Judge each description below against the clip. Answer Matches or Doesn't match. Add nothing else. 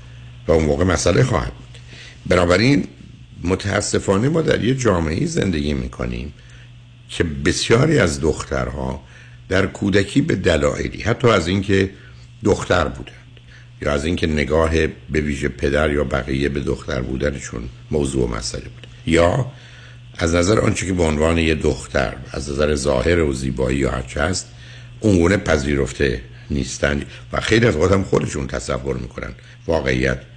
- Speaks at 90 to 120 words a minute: Doesn't match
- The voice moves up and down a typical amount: Doesn't match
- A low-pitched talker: Matches